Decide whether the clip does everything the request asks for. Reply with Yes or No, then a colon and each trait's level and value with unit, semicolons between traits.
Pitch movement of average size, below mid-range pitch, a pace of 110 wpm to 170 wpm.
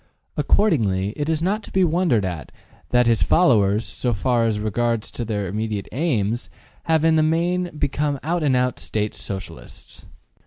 No: wide, 7.2 semitones; low, 125 Hz; average, 160 wpm